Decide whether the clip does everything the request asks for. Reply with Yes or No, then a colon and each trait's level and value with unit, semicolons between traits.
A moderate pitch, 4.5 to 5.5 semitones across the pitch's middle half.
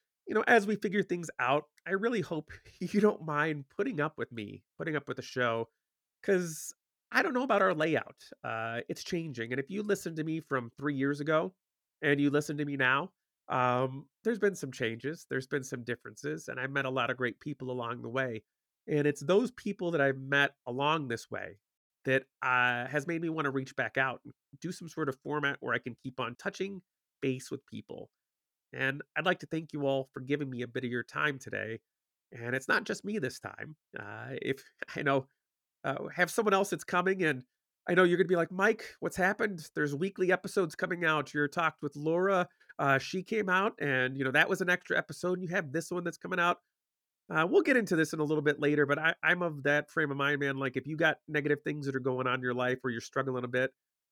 Yes: medium, 150 Hz; average, 5.0 semitones